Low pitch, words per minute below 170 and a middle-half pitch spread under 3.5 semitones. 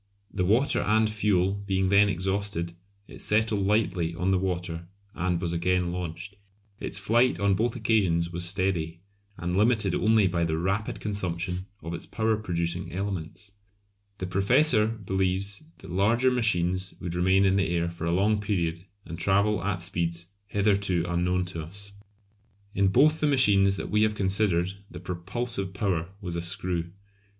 Yes: very low, 95 Hz; average, 160 wpm; average, 2.9 semitones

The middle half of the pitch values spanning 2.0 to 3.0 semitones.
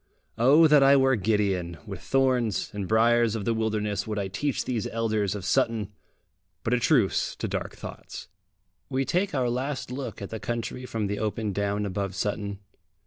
No: average, 3.8 semitones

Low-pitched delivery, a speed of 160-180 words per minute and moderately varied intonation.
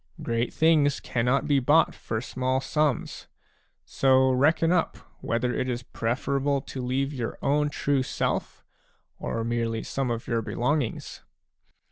No: low, 130 Hz; slow, 135 wpm; average, 3.1 semitones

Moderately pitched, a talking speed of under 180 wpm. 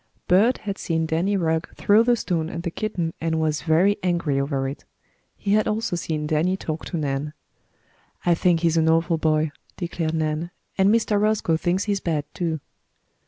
No: medium, 165 Hz; average, 185 wpm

